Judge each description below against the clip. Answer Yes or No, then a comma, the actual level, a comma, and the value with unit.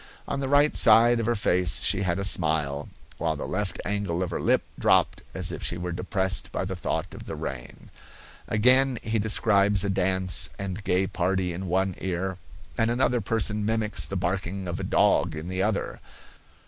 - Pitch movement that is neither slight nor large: Yes, average, 3.2 semitones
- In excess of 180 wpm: Yes, average, 190 wpm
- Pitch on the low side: Yes, very low, 95 Hz